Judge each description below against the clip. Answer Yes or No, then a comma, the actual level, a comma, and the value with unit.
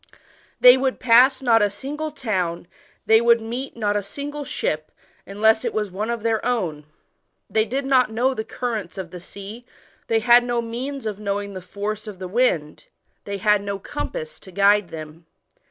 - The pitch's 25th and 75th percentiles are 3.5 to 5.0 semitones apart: Yes, average, 3.8 semitones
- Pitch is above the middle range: Yes, high, 220 Hz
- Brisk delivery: No, average, 185 wpm